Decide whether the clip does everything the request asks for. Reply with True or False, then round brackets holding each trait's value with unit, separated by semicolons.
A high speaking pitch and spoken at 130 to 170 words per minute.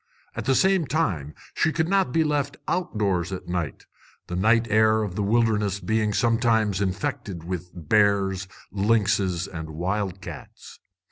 False (105 Hz; 145 wpm)